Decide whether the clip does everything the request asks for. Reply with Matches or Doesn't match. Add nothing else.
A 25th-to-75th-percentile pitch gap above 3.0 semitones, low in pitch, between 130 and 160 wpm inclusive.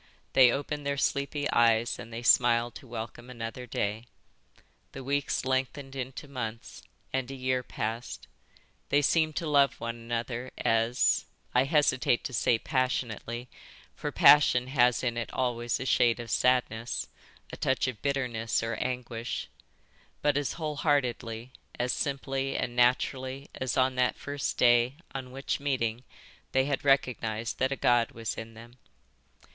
Doesn't match